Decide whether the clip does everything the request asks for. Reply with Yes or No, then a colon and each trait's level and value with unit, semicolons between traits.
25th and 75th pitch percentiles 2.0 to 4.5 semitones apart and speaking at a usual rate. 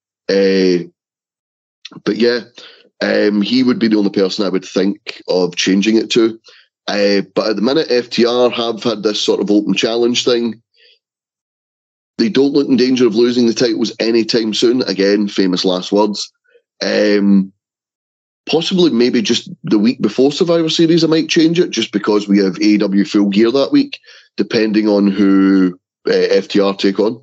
Yes: average, 3.9 semitones; average, 165 wpm